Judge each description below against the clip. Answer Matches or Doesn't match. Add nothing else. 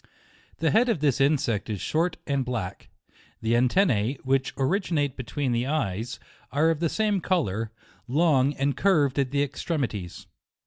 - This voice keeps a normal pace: Matches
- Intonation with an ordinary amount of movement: Matches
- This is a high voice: Doesn't match